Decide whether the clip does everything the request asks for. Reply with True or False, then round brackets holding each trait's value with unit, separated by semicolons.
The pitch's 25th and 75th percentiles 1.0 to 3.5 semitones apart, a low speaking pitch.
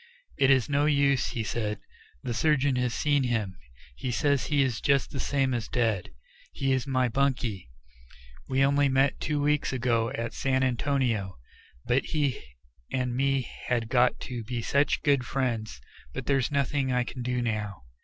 True (2.8 semitones; 130 Hz)